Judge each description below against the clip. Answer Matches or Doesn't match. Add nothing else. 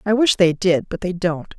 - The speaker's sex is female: Matches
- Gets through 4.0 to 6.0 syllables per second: Matches